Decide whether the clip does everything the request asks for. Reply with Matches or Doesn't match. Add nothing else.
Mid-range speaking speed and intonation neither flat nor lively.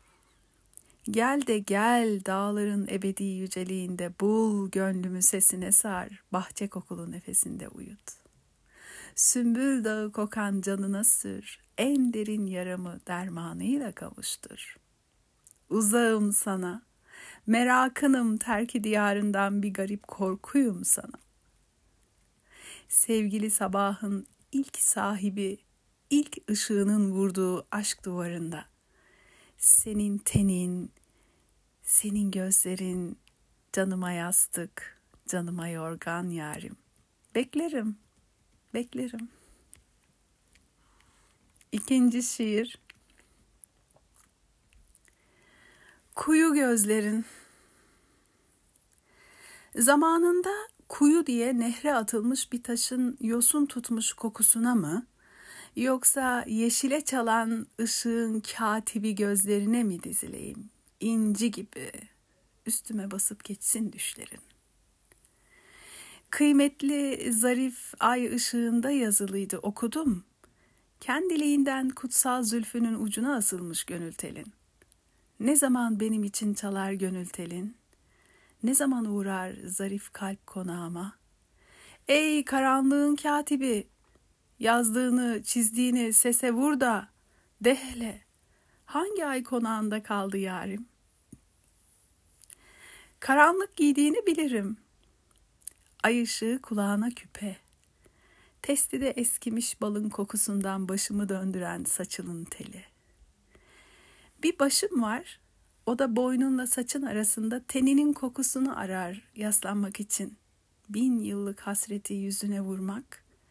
Doesn't match